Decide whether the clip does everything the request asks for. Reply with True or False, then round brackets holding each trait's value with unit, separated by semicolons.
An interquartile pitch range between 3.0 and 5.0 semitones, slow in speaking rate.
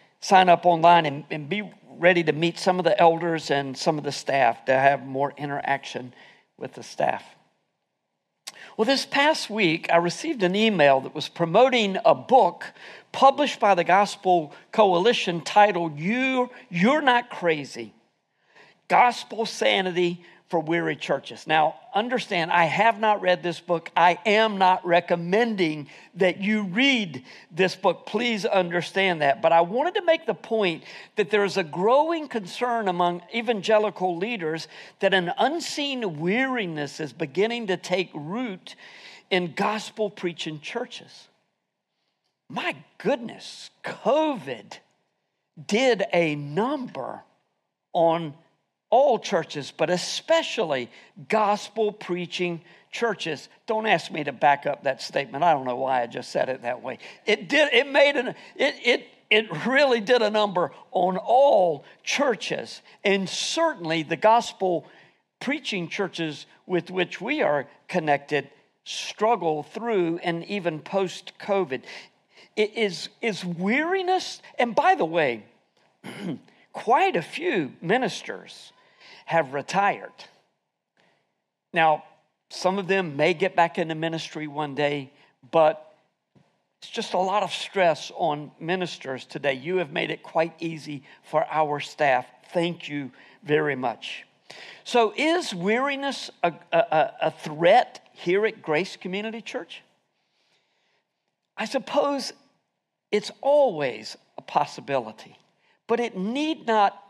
False (5.4 semitones; 130 wpm)